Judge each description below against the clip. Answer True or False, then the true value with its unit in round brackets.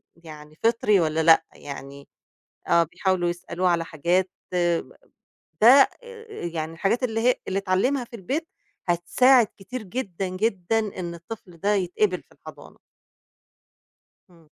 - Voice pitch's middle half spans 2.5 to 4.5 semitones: False (4.9 semitones)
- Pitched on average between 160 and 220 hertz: True (185 Hz)